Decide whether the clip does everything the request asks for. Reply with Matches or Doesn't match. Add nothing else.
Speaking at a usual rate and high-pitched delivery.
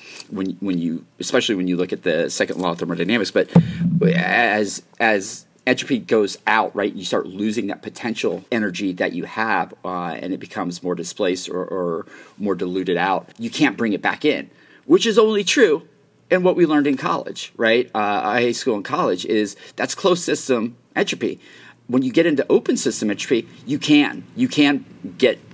Doesn't match